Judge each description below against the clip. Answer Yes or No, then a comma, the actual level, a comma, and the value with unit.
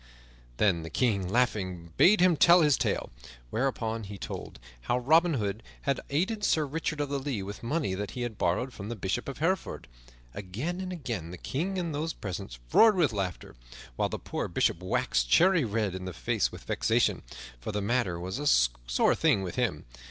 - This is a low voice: Yes, low, 120 Hz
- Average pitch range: No, wide, 8.3 semitones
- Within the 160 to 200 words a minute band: Yes, average, 195 wpm